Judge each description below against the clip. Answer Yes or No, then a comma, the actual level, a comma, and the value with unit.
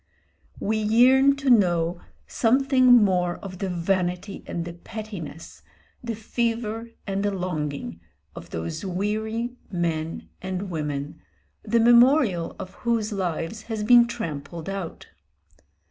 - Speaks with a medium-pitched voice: No, high, 195 Hz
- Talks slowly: Yes, slow, 120 wpm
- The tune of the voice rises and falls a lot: No, average, 5.0 semitones